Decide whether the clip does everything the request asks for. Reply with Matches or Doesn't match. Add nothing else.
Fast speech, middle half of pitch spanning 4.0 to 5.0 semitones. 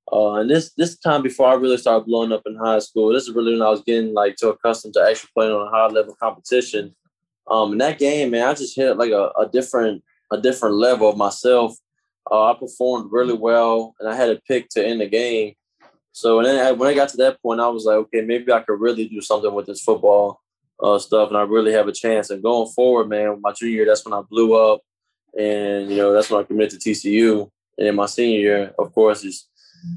Doesn't match